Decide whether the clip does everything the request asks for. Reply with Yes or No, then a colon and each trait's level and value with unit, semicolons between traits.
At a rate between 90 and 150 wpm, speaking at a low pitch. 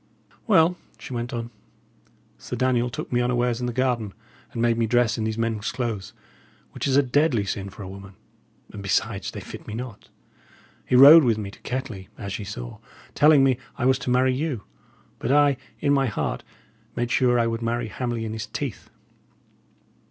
No: average, 190 wpm; low, 120 Hz